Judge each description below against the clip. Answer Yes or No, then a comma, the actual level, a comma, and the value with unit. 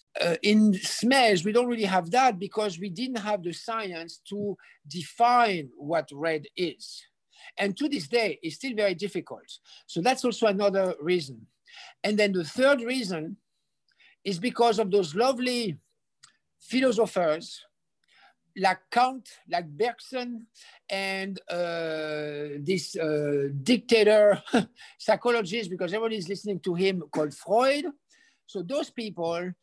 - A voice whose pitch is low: No, high, 200 Hz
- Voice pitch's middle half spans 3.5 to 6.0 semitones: Yes, average, 5.3 semitones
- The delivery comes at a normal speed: No, slow, 130 wpm